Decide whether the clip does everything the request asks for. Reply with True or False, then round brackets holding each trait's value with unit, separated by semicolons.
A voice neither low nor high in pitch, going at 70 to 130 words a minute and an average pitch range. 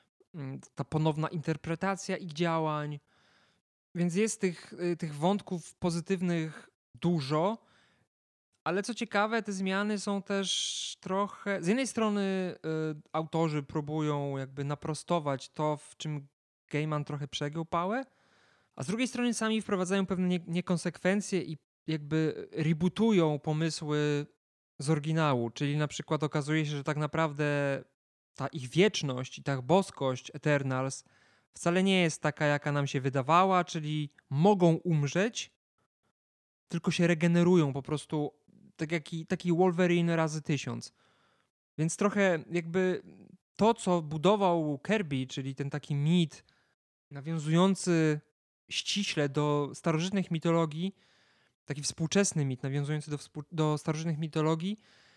True (160 Hz; 120 wpm; 3.8 semitones)